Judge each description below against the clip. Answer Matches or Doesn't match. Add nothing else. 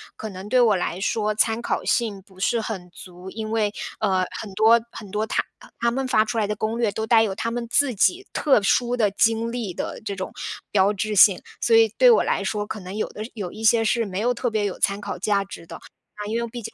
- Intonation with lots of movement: Doesn't match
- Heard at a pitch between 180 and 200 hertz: Doesn't match